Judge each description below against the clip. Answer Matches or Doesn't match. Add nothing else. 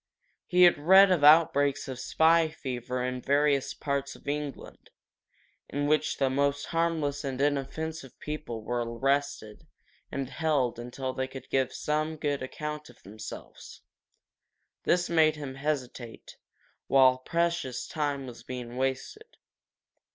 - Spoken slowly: Matches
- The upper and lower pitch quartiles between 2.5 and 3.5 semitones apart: Matches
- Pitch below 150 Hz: Matches